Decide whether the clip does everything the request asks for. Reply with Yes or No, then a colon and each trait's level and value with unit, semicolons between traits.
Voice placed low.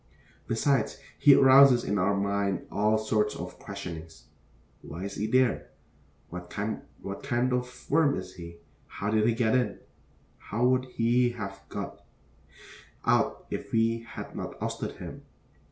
Yes: low, 110 Hz